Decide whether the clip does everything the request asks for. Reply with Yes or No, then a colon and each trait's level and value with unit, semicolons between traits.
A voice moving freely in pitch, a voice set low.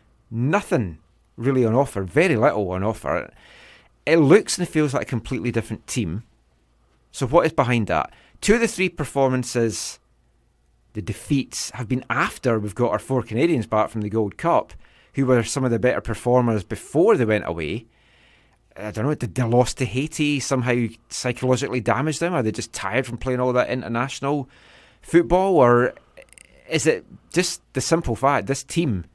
No: average, 3.8 semitones; low, 125 Hz